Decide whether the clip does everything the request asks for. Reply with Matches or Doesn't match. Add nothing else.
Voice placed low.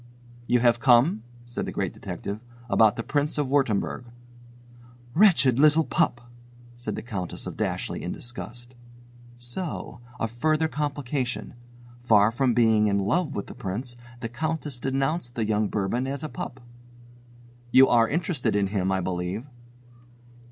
Matches